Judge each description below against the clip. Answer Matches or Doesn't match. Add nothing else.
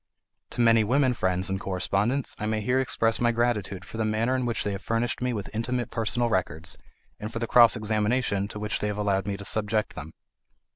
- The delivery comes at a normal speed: Doesn't match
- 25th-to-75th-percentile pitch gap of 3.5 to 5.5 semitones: Doesn't match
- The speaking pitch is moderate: Doesn't match